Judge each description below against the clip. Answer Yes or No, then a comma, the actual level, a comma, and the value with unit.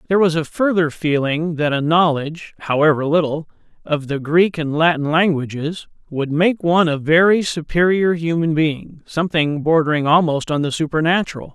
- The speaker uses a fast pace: No, average, 155 wpm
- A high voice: No, medium, 160 Hz